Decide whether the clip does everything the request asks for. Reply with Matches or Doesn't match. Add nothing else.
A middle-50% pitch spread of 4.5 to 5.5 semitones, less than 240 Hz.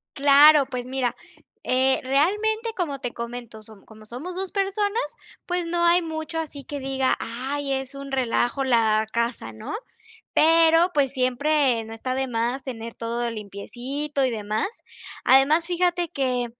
Doesn't match